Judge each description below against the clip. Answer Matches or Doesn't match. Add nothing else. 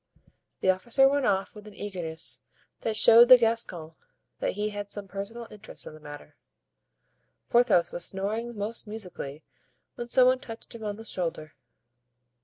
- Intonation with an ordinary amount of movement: Matches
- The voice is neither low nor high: Doesn't match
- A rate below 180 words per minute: Matches